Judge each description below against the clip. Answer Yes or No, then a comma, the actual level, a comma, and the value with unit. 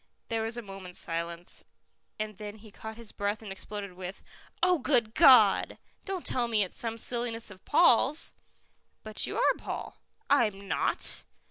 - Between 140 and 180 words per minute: Yes, average, 160 wpm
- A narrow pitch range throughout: No, average, 3.3 semitones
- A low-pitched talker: No, high, 220 Hz